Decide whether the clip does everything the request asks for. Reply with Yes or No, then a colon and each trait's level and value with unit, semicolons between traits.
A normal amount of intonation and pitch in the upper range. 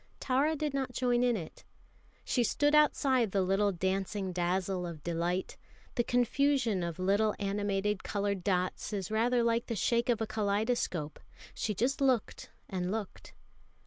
Yes: average, 4.5 semitones; high, 210 Hz